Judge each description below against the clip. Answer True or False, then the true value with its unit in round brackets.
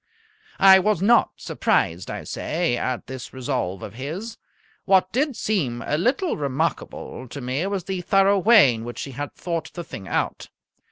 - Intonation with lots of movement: True (7.2 semitones)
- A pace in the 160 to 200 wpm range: True (170 wpm)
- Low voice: False (165 Hz)